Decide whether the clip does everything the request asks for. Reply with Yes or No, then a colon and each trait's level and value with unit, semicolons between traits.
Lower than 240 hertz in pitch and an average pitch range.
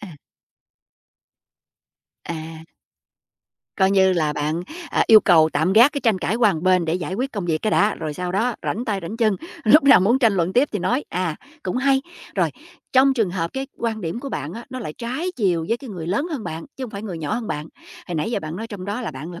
No: high, 200 Hz; wide, 5.8 semitones